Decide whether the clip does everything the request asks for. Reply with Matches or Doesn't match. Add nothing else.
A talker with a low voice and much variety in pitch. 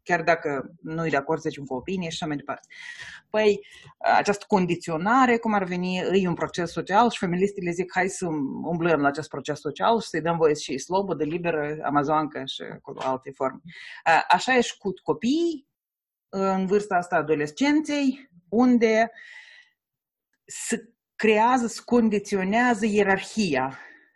Doesn't match